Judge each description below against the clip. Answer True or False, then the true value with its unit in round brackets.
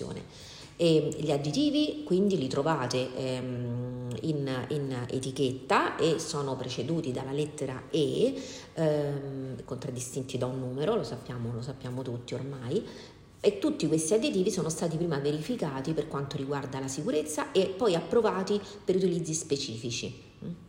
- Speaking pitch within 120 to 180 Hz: True (140 Hz)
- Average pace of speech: True (135 wpm)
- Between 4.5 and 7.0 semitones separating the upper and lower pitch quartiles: False (3.7 semitones)